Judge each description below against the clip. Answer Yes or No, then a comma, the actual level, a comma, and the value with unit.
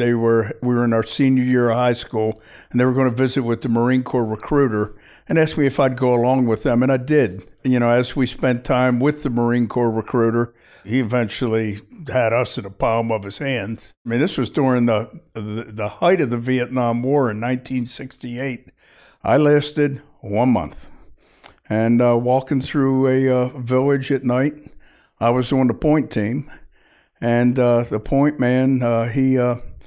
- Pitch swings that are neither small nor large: No, narrow, 2.2 semitones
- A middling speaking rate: Yes, average, 195 wpm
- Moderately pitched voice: No, low, 125 Hz